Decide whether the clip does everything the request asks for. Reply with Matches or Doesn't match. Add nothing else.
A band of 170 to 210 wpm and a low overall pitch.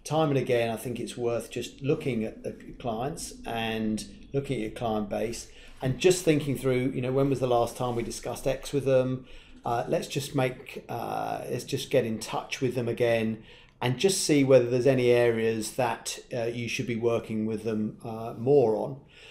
Matches